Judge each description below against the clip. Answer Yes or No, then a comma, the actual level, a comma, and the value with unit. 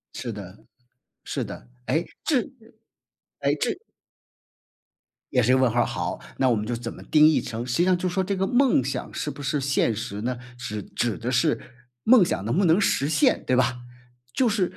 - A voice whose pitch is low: Yes, low, 130 Hz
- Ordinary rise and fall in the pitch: No, wide, 6.9 semitones